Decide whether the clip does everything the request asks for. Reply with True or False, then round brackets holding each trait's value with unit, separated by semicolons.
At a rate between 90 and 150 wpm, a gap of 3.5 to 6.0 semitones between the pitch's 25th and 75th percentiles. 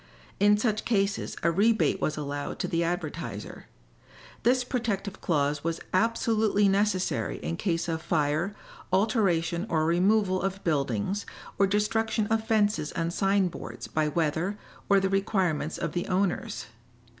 True (140 wpm; 3.9 semitones)